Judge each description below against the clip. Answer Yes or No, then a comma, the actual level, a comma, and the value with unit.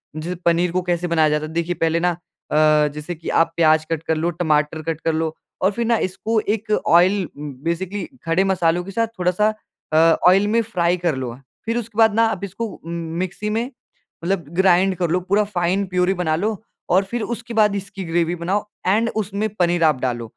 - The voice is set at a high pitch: No, medium, 180 Hz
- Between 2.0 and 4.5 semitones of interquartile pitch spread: Yes, average, 3.5 semitones